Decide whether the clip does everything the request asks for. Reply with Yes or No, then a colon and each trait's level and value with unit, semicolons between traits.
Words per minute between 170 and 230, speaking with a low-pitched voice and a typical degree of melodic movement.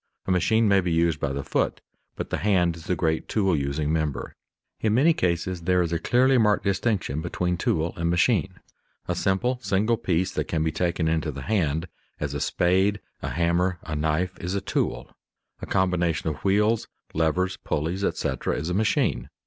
Yes: average, 190 wpm; very low, 90 Hz; average, 3.4 semitones